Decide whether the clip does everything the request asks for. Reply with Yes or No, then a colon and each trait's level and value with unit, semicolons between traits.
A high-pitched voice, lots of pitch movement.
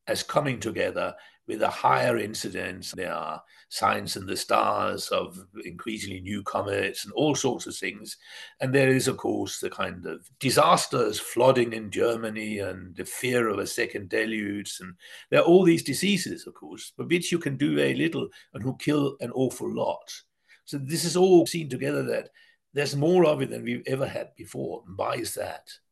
No: low, 130 Hz; wide, 7.0 semitones